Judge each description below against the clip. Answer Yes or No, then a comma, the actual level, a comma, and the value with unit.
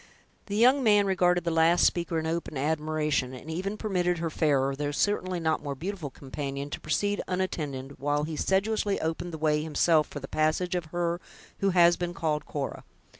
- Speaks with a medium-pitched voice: Yes, medium, 160 Hz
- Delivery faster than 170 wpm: Yes, average, 185 wpm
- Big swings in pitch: No, average, 3.3 semitones